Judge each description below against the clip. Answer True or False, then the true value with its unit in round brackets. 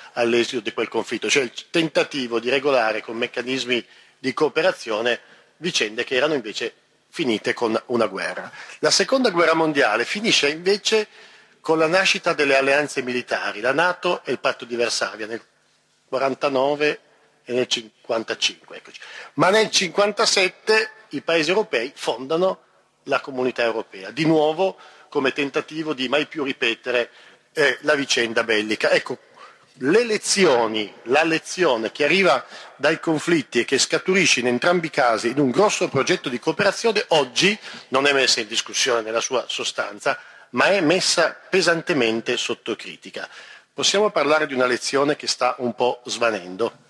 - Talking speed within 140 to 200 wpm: True (145 wpm)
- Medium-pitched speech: True (145 Hz)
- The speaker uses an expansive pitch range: True (6.3 semitones)